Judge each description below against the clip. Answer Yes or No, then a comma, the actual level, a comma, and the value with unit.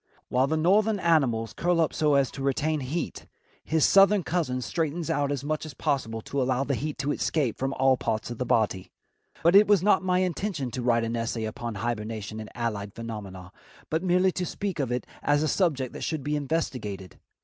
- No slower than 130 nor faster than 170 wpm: No, fast, 205 wpm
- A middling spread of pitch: No, wide, 5.8 semitones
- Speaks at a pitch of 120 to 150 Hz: Yes, medium, 140 Hz